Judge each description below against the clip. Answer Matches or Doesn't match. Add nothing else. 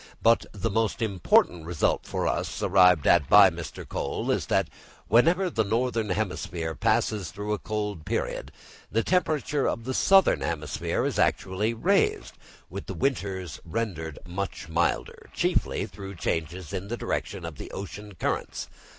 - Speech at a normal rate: Matches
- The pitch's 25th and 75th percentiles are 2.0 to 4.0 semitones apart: Doesn't match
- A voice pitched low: Matches